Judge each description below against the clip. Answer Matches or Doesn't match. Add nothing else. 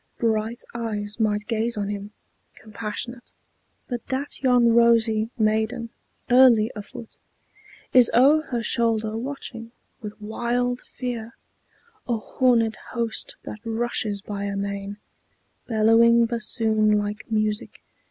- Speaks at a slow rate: Matches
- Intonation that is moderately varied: Doesn't match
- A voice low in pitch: Doesn't match